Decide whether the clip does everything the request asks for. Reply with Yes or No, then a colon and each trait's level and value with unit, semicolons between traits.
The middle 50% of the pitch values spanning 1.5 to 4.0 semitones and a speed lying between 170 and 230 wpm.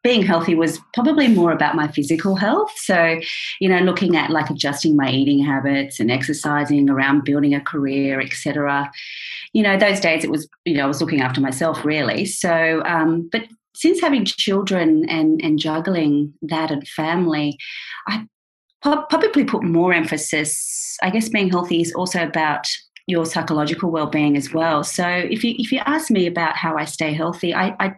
No: average, 4.5 semitones; average, 180 wpm